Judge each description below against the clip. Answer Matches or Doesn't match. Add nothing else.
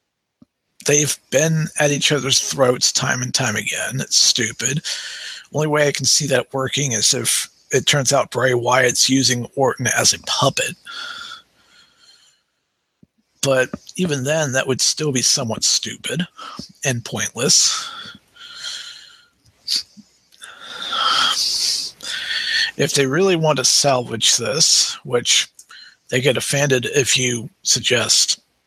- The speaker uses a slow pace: Matches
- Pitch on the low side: Doesn't match